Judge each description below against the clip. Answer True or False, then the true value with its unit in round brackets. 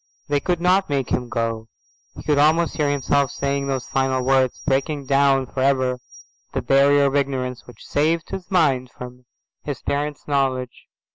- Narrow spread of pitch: True (2.1 semitones)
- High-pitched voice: False (140 Hz)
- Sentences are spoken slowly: False (165 wpm)